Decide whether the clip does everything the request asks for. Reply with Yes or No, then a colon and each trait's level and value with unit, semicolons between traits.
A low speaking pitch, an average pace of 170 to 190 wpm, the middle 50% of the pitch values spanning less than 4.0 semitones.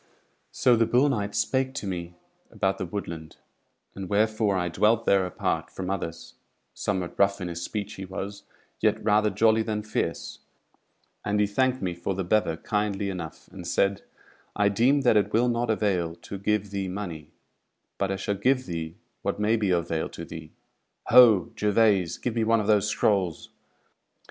Yes: low, 100 Hz; average, 180 wpm; average, 3.0 semitones